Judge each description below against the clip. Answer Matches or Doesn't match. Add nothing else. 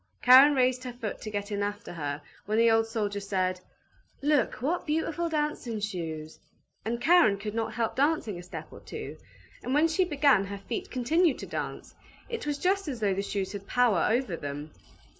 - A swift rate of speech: Doesn't match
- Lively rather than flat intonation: Matches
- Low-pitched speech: Doesn't match